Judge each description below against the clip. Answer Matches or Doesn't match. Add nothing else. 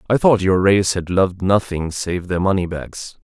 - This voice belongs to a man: Matches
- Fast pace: Doesn't match